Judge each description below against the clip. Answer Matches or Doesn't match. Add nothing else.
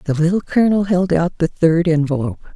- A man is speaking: Doesn't match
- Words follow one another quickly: Doesn't match